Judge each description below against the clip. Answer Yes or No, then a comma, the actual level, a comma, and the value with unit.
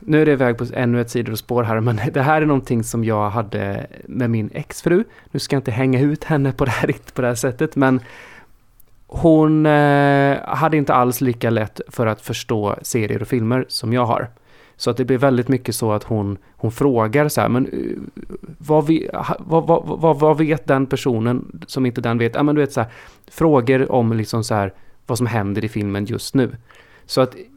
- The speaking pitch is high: No, low, 125 Hz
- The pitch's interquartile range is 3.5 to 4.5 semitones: Yes, average, 3.9 semitones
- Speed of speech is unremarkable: No, fast, 215 wpm